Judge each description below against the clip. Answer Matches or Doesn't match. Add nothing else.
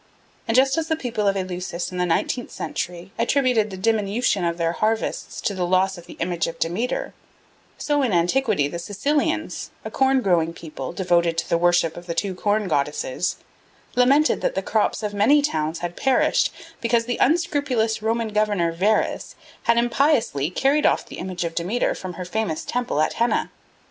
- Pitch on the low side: Doesn't match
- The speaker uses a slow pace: Doesn't match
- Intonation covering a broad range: Matches